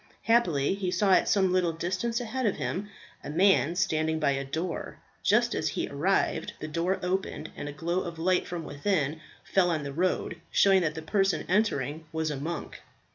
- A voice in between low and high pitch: Yes, medium, 175 Hz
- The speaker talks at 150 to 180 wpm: No, average, 190 wpm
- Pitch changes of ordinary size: Yes, average, 3.6 semitones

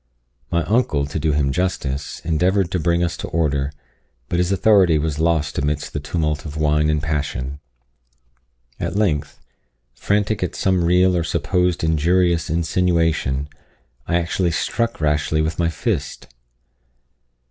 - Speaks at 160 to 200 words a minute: No, average, 140 wpm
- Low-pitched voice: Yes, very low, 80 Hz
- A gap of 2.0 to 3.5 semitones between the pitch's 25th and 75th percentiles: Yes, average, 3.2 semitones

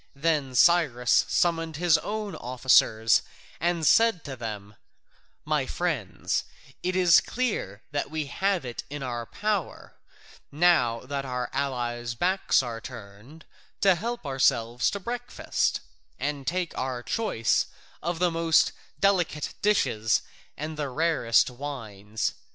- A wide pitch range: Yes, wide, 6.3 semitones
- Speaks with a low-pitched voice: No, medium, 145 Hz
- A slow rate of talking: Yes, slow, 125 wpm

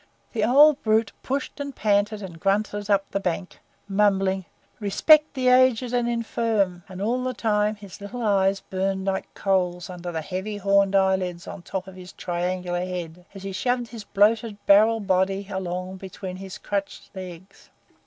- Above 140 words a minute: Yes, average, 170 wpm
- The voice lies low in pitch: No, high, 195 Hz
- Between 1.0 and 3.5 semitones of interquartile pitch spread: Yes, average, 2.7 semitones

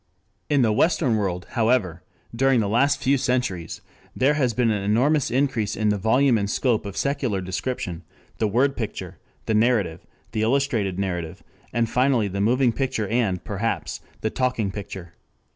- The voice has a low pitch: Yes, low, 115 Hz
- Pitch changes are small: No, average, 4.4 semitones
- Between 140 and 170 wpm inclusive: Yes, average, 160 wpm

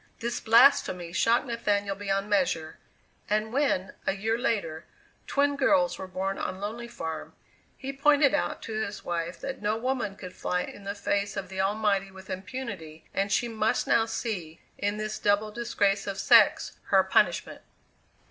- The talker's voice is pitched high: Yes, high, 205 Hz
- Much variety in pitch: No, average, 3.3 semitones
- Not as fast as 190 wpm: Yes, average, 165 wpm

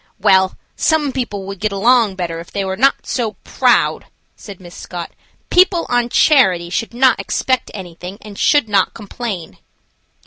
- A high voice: Yes, high, 205 Hz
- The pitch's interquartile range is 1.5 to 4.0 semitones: No, average, 4.8 semitones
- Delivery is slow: No, average, 160 wpm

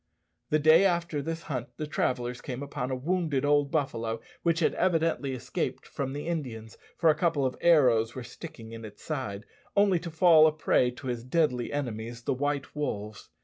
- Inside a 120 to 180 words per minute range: No, average, 190 wpm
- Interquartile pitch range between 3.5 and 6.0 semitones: Yes, average, 4.7 semitones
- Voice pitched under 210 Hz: Yes, medium, 140 Hz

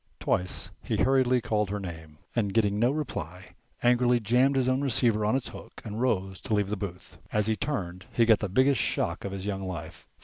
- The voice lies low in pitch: Yes, low, 105 Hz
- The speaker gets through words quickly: Yes, fast, 210 wpm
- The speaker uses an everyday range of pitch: Yes, average, 4.3 semitones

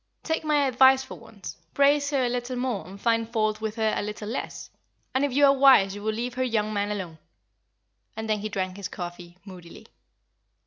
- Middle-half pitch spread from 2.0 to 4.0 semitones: No, average, 4.5 semitones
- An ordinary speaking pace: No, fast, 210 wpm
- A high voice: Yes, high, 220 Hz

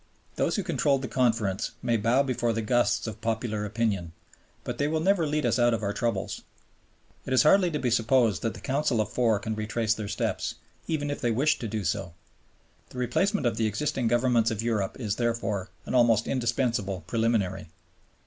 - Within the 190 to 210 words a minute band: Yes, average, 195 wpm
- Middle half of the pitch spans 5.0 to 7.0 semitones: No, average, 3.1 semitones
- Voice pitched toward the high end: No, low, 115 Hz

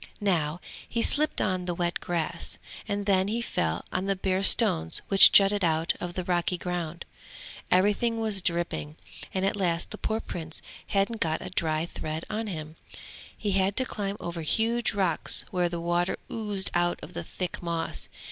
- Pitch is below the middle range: No, medium, 180 Hz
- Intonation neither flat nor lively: Yes, average, 3.2 semitones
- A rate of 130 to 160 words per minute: No, average, 175 wpm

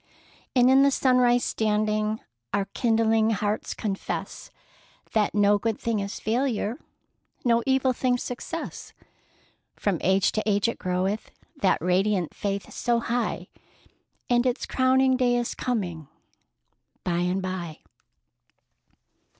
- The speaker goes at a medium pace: No, slow, 120 wpm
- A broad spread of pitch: No, average, 3.8 semitones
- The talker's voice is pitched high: Yes, high, 220 Hz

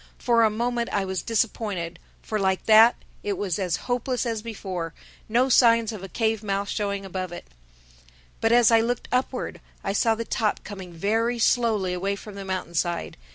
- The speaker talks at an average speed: Yes, average, 175 wpm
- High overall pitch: Yes, high, 210 Hz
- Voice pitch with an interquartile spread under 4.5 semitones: Yes, average, 3.3 semitones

